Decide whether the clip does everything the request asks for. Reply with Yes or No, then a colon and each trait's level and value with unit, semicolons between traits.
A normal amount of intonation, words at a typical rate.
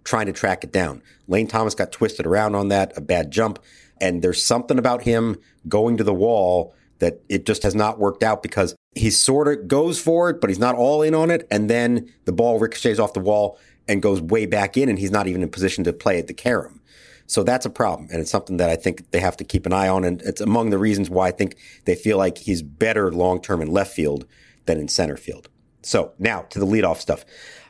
No: average, 3.5 semitones; fast, 245 wpm